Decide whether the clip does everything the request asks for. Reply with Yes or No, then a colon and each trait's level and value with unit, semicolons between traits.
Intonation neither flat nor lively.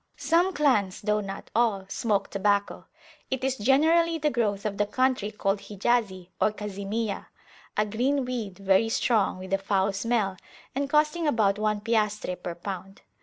Yes: average, 4.2 semitones